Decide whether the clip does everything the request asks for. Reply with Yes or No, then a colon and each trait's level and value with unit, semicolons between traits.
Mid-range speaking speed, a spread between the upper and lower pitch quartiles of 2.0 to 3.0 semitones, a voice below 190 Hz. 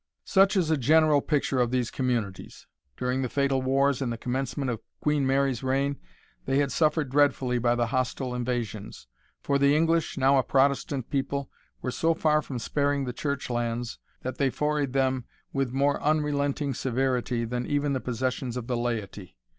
Yes: average, 175 wpm; narrow, 2.5 semitones; low, 135 Hz